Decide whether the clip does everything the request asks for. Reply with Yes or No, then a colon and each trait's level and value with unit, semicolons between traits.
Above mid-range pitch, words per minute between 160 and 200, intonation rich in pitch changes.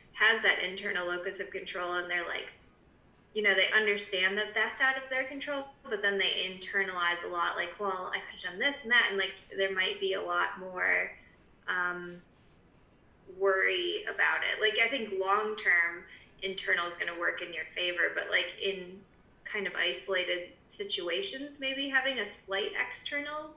Yes: high, 195 Hz; average, 180 wpm; wide, 6.2 semitones